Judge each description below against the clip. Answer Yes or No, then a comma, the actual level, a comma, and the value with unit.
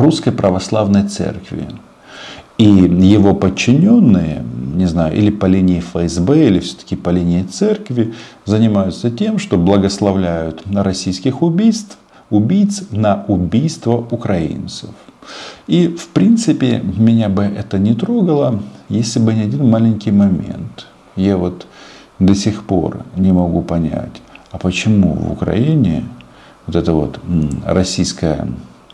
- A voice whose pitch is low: Yes, low, 100 Hz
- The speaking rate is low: No, average, 120 wpm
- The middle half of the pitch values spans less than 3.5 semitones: No, average, 4.3 semitones